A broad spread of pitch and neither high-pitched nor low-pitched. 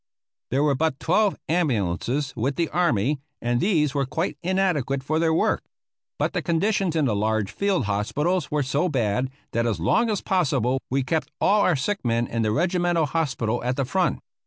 Yes: wide, 6.1 semitones; medium, 145 Hz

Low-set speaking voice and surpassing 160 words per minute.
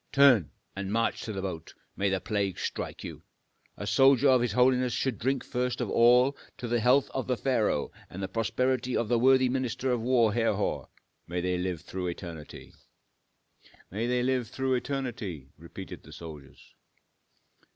Yes: low, 115 Hz; average, 170 wpm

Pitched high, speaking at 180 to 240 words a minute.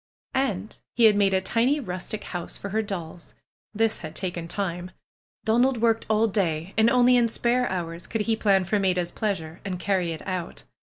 Yes: high, 200 Hz; average, 185 wpm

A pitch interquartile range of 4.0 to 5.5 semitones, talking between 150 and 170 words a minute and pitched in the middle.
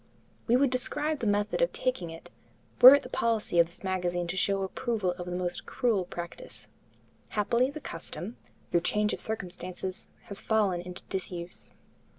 No: average, 4.8 semitones; average, 165 wpm; high, 195 Hz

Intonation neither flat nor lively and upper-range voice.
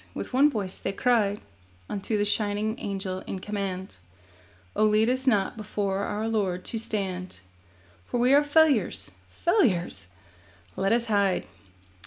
Yes: average, 3.3 semitones; high, 210 Hz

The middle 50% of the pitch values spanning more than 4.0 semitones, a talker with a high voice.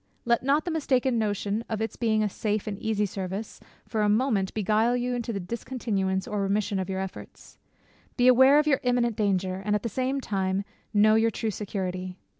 No: average, 3.6 semitones; high, 215 Hz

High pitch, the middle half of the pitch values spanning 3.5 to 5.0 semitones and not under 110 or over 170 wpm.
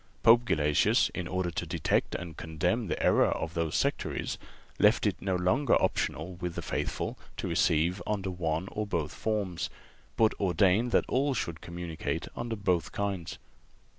No: very low, 90 Hz; average, 4.0 semitones; average, 160 wpm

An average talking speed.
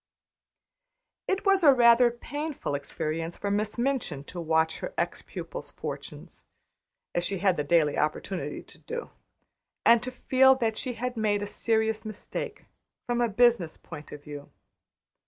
Yes: average, 155 wpm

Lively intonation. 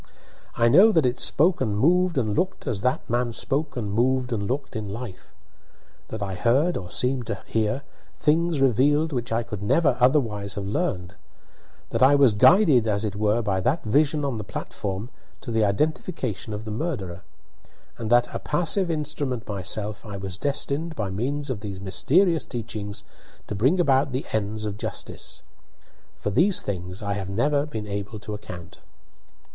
Yes: wide, 5.7 semitones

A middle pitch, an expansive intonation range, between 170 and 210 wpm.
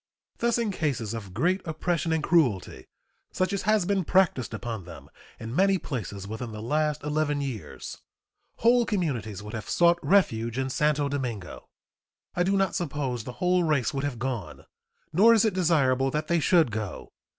Yes: medium, 145 Hz; wide, 7.4 semitones; average, 175 wpm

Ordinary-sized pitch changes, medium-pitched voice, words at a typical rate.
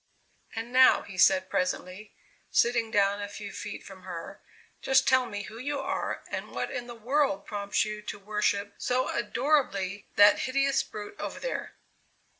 No: average, 4.0 semitones; high, 210 Hz; average, 165 wpm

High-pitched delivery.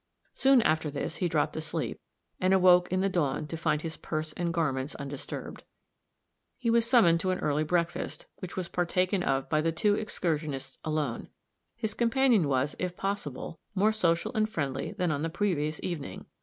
No: medium, 170 Hz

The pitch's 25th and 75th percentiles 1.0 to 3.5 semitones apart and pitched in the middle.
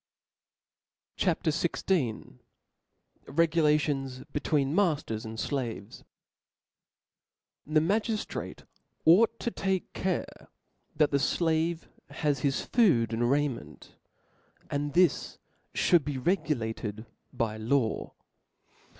No: average, 5.2 semitones; medium, 145 Hz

